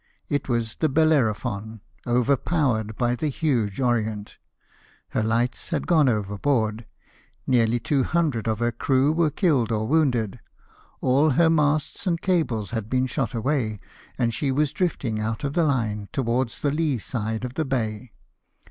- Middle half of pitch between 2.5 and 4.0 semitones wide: No, average, 4.8 semitones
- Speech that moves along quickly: No, average, 150 wpm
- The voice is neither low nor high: No, low, 125 Hz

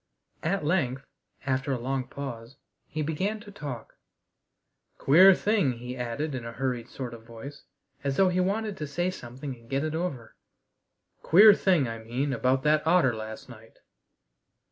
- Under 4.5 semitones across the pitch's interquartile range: No, wide, 5.6 semitones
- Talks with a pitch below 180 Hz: Yes, low, 135 Hz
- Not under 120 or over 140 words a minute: No, average, 165 wpm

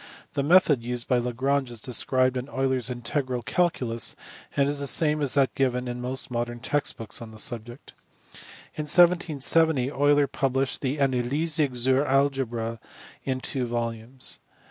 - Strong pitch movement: No, average, 2.8 semitones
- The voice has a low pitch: Yes, low, 130 Hz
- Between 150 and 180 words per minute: Yes, average, 155 wpm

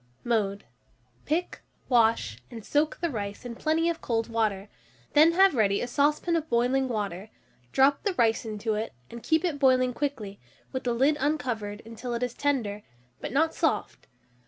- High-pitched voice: Yes, high, 245 Hz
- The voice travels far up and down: No, average, 5.0 semitones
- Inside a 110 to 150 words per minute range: No, average, 170 wpm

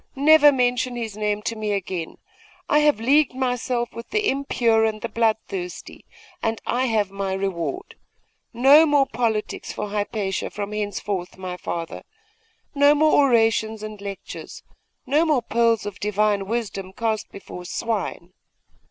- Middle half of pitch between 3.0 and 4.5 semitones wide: Yes, average, 4.0 semitones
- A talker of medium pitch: No, high, 225 Hz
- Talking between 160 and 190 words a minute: No, average, 145 wpm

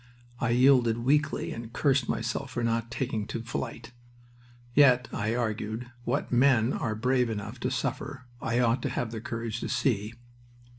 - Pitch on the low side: Yes, low, 120 Hz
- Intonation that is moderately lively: No, narrow, 2.1 semitones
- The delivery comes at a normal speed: Yes, average, 160 wpm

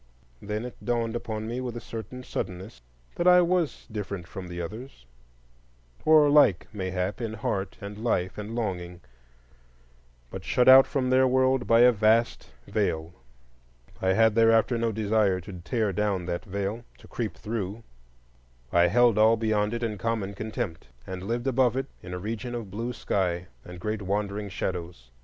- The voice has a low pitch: Yes, low, 110 Hz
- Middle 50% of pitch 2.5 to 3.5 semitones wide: No, average, 3.9 semitones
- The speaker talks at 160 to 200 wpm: Yes, average, 165 wpm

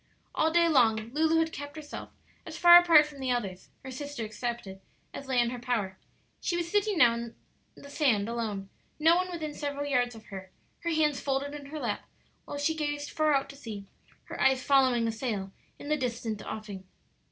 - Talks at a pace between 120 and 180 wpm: No, average, 200 wpm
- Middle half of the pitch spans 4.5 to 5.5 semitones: Yes, average, 4.9 semitones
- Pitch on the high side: Yes, very high, 270 Hz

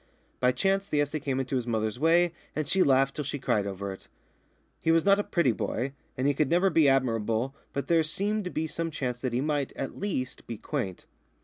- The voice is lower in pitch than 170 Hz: Yes, medium, 140 Hz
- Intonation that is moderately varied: Yes, average, 4.8 semitones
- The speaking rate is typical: No, fast, 225 wpm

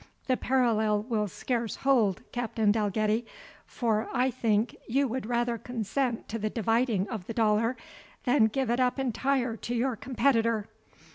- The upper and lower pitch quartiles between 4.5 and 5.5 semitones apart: No, narrow, 2.6 semitones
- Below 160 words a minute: Yes, average, 150 wpm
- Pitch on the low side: No, high, 230 Hz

